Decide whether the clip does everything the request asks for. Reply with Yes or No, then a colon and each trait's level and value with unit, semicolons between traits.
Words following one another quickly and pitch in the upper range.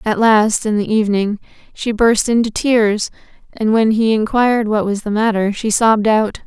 No: average, 185 wpm; high, 215 Hz